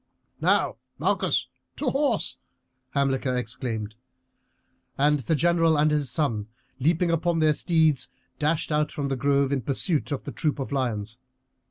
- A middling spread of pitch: Yes, average, 3.7 semitones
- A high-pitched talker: No, medium, 145 Hz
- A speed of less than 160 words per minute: Yes, average, 145 wpm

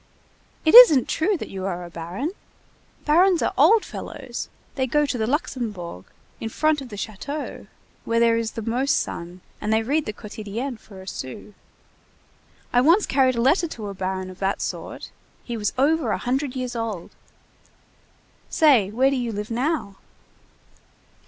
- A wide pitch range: Yes, wide, 5.7 semitones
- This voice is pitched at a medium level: No, high, 235 Hz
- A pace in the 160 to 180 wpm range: Yes, average, 170 wpm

